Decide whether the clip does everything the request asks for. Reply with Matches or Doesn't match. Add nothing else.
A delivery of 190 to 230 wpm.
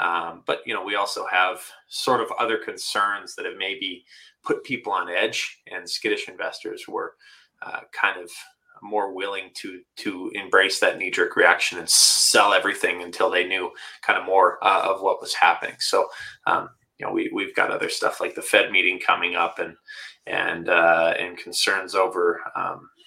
Doesn't match